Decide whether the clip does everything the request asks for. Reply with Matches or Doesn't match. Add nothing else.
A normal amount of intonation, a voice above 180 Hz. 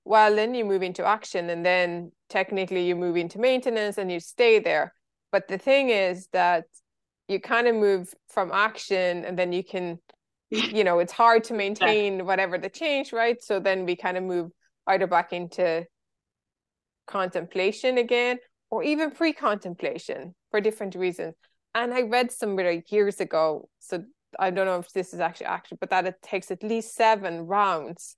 Matches